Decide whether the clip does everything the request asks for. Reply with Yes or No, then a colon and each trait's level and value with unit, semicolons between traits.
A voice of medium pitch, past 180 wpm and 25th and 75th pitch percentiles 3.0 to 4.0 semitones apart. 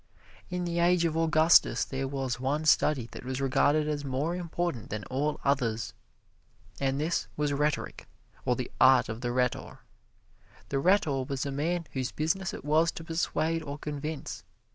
No: medium, 145 Hz; average, 165 wpm; average, 3.6 semitones